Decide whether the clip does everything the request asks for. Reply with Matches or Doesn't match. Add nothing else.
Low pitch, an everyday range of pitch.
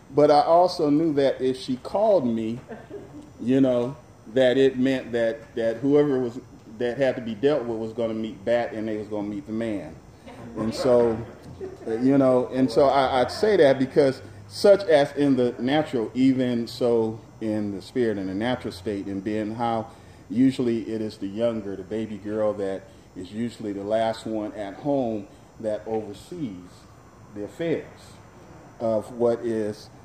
Matches